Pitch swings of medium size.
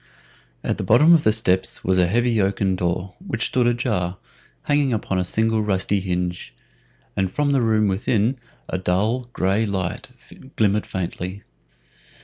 Yes: average, 4.1 semitones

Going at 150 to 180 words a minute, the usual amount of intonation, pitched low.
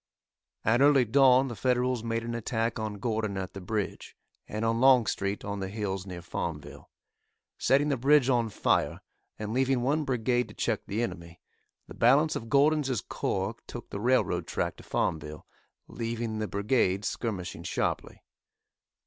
Yes: average, 155 wpm; average, 4.1 semitones; low, 115 Hz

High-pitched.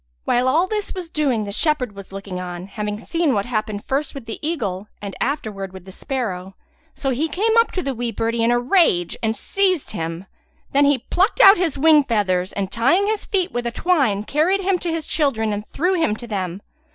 Yes: high, 245 Hz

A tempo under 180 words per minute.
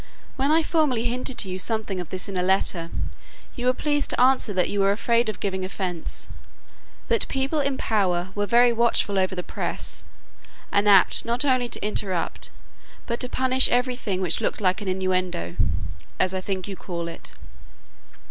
No: average, 185 wpm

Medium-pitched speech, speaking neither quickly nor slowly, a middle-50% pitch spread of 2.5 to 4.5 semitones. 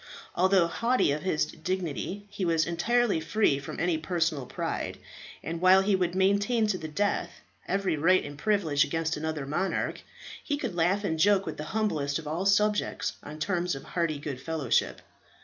Yes: medium, 175 Hz; average, 175 wpm; average, 4.1 semitones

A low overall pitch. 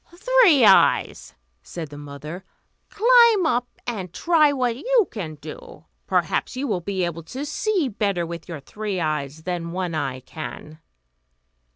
No: high, 195 Hz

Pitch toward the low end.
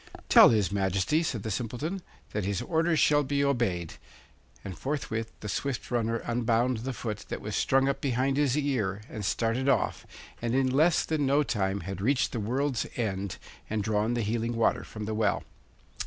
Yes: low, 115 Hz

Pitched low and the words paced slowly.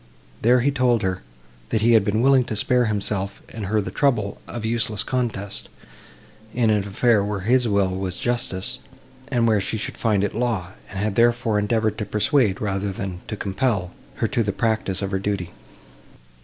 No: low, 105 Hz; average, 185 wpm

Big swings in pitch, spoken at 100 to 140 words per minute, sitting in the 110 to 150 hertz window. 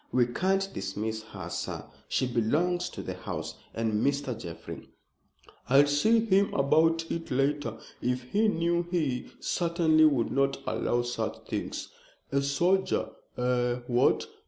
Yes: wide, 5.7 semitones; slow, 135 wpm; medium, 140 Hz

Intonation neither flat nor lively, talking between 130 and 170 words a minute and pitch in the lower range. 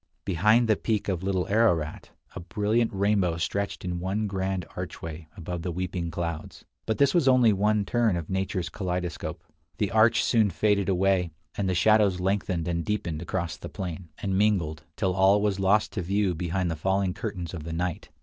No: average, 3.1 semitones; average, 185 wpm; very low, 95 Hz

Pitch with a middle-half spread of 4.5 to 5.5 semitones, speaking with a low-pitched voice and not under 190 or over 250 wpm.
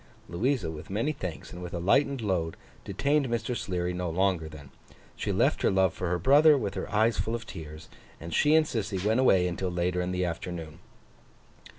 Yes: average, 5.1 semitones; very low, 95 Hz; average, 200 wpm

